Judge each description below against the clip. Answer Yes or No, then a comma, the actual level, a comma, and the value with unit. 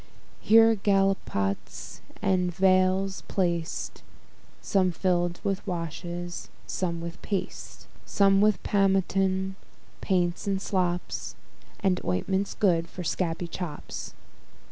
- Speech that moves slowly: Yes, slow, 100 wpm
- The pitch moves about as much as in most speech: No, narrow, 2.1 semitones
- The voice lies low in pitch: No, medium, 185 Hz